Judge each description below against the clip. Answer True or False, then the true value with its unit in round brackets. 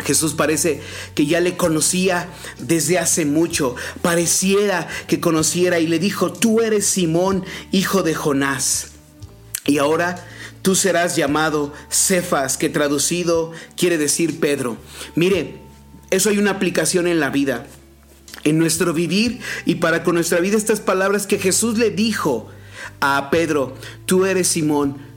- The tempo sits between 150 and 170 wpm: False (140 wpm)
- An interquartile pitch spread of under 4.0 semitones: False (4.4 semitones)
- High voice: False (170 Hz)